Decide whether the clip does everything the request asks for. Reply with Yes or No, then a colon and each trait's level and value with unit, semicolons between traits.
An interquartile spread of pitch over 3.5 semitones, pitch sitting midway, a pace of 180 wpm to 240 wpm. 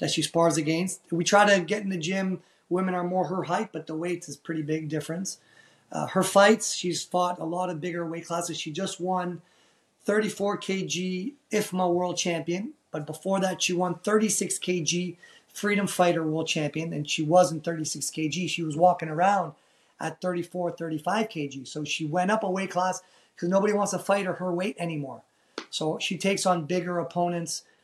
No: narrow, 2.4 semitones; medium, 180 Hz; average, 190 wpm